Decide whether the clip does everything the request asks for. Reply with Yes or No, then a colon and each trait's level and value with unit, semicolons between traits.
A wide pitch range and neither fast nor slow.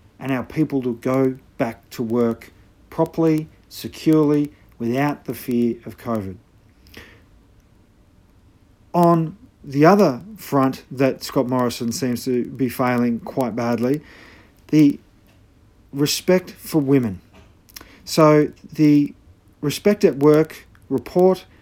No: wide, 6.3 semitones; slow, 105 wpm